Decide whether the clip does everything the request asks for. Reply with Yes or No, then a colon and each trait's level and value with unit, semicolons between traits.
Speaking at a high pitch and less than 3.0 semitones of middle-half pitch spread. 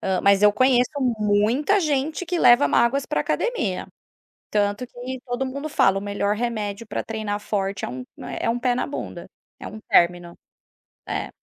No: high, 225 Hz; average, 4.3 semitones